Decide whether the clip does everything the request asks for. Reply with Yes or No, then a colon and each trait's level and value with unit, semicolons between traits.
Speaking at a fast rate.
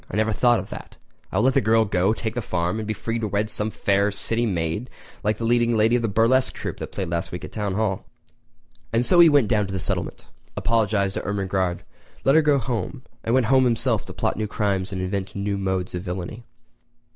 Yes: fast, 240 wpm